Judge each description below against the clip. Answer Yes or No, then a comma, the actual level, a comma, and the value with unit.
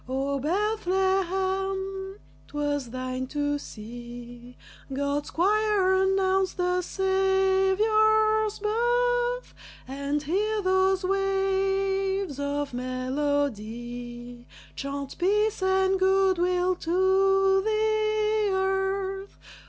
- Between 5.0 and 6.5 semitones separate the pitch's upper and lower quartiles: Yes, average, 5.3 semitones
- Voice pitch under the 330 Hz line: No, very high, 380 Hz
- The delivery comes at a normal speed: No, slow, 80 wpm